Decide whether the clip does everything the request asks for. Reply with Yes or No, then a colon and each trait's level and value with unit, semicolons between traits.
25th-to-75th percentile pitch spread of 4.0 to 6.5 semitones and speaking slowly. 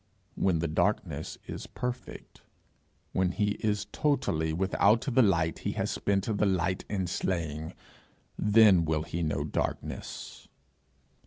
Yes: average, 4.3 semitones; slow, 130 wpm